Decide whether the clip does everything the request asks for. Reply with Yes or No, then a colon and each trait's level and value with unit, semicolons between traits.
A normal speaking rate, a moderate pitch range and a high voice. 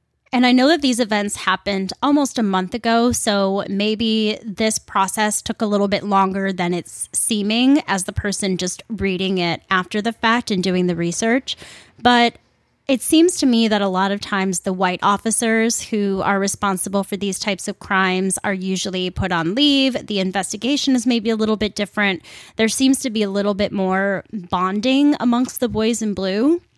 Yes: average, 190 wpm; average, 3.2 semitones; high, 205 Hz